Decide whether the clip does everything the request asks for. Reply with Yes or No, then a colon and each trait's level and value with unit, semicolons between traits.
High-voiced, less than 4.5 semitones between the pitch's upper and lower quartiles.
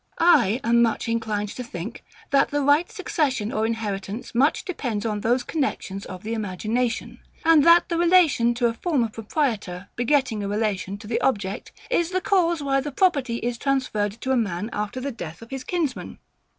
No: high, 235 Hz; wide, 5.4 semitones